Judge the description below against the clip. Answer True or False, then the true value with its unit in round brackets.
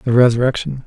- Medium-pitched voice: False (125 Hz)